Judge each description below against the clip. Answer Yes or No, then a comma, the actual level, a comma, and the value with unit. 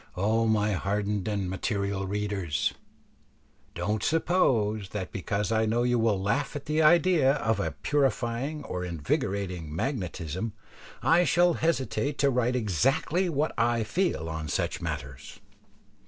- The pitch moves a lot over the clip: Yes, wide, 6.2 semitones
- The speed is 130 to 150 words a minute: Yes, slow, 135 wpm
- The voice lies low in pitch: Yes, low, 110 Hz